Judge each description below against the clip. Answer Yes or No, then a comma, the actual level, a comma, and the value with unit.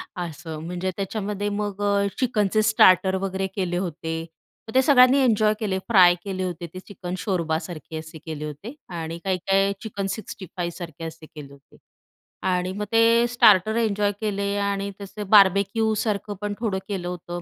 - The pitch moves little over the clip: No, average, 3.0 semitones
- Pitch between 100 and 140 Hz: No, high, 195 Hz